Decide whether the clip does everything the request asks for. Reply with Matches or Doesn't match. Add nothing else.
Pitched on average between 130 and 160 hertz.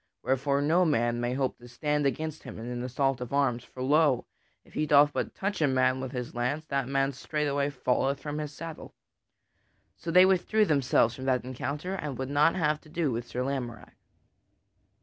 Matches